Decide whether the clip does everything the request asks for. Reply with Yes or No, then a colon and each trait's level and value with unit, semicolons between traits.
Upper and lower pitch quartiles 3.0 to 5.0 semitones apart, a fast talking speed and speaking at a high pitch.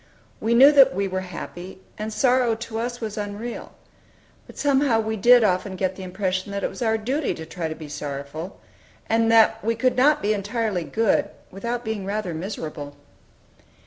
No: average, 3.9 semitones; average, 180 wpm; high, 215 Hz